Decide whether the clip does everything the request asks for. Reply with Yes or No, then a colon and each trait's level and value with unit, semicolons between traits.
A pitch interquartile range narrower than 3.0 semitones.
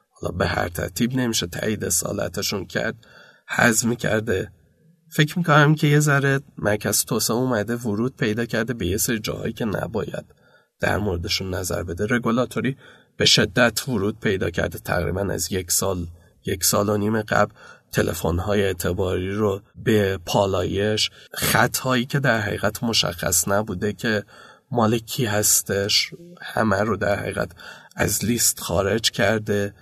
No: average, 3.9 semitones